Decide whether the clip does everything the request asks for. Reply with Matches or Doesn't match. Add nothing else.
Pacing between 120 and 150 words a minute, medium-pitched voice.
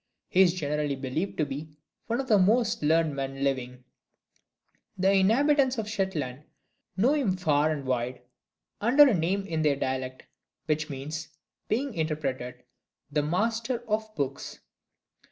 Matches